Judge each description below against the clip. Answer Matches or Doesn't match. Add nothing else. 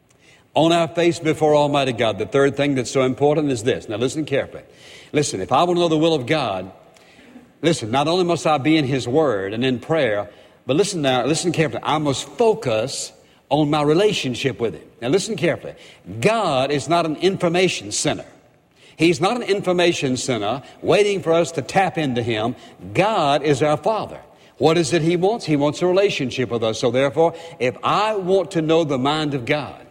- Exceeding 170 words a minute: Matches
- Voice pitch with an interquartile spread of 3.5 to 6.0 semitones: Matches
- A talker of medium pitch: Matches